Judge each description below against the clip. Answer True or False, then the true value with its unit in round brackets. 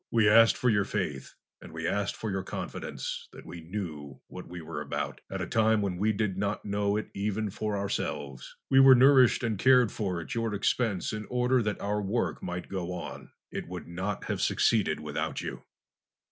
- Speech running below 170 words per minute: False (200 wpm)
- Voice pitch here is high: False (100 Hz)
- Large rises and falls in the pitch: False (3.7 semitones)